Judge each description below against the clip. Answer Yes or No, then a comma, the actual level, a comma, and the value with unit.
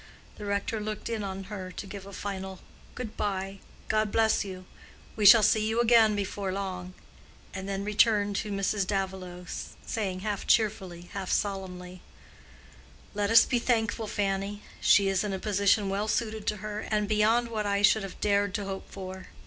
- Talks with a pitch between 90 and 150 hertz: No, high, 200 Hz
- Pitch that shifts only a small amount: Yes, narrow, 1.9 semitones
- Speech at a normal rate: Yes, average, 175 wpm